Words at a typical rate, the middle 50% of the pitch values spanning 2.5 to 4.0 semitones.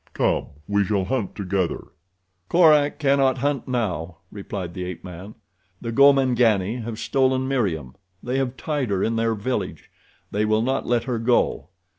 No: average, 155 wpm; average, 5.0 semitones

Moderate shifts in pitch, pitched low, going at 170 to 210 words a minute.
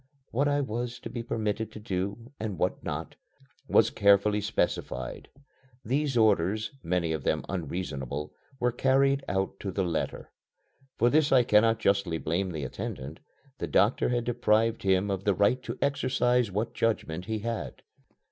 No: average, 4.4 semitones; low, 105 Hz; average, 155 wpm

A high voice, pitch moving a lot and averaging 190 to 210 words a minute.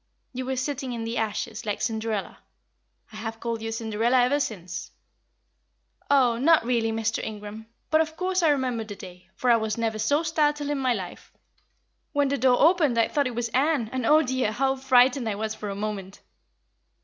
No: high, 240 Hz; average, 4.0 semitones; average, 195 wpm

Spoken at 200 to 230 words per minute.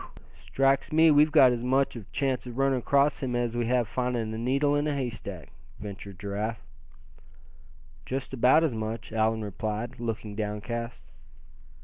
No: average, 155 wpm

